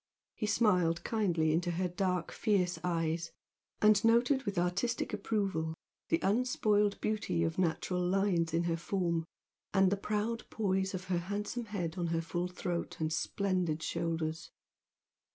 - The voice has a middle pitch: Yes, medium, 180 Hz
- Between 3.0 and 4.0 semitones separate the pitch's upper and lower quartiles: Yes, average, 3.6 semitones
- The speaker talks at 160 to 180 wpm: No, average, 145 wpm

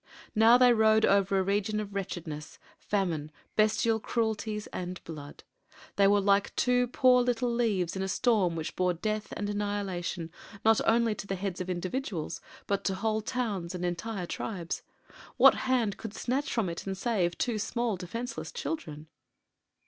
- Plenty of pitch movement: No, average, 3.8 semitones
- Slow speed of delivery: No, average, 165 wpm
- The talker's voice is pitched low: No, high, 205 Hz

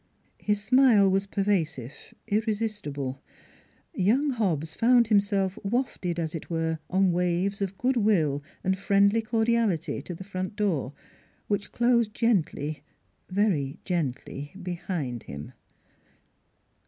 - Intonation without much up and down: No, average, 4.7 semitones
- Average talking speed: No, slow, 115 wpm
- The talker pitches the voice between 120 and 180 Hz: No, high, 195 Hz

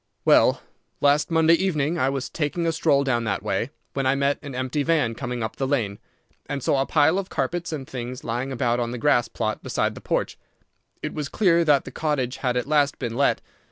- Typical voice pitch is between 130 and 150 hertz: Yes, medium, 140 Hz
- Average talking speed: No, fast, 220 wpm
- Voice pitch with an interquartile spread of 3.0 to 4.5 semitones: Yes, average, 3.6 semitones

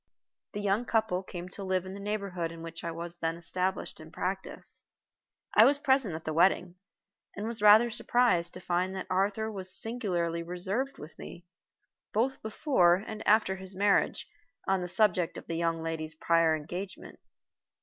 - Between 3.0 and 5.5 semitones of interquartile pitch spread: Yes, average, 3.8 semitones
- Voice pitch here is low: No, medium, 185 Hz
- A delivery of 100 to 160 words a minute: No, average, 170 wpm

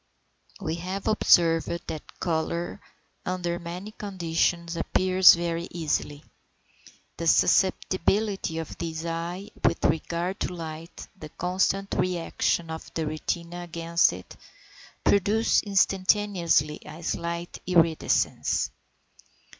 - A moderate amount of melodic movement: No, narrow, 2.1 semitones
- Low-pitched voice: No, medium, 170 Hz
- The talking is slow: Yes, slow, 105 wpm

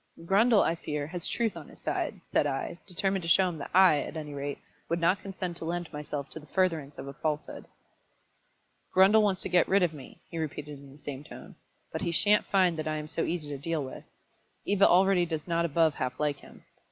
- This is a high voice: No, medium, 165 Hz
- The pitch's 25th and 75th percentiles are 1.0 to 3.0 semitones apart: No, average, 3.8 semitones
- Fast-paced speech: Yes, fast, 225 wpm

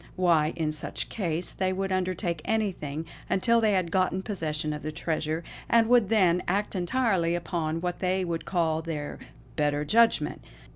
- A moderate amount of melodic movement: Yes, average, 3.4 semitones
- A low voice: No, medium, 175 Hz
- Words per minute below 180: Yes, average, 160 wpm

